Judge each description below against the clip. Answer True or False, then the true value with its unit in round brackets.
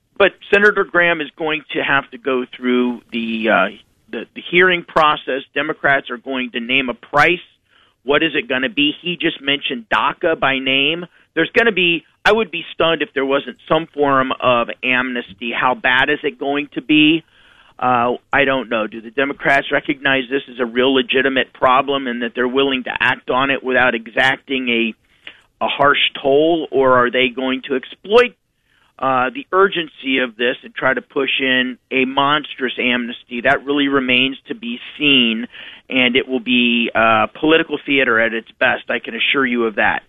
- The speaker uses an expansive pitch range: False (3.4 semitones)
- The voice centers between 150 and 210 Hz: False (135 Hz)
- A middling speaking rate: True (190 wpm)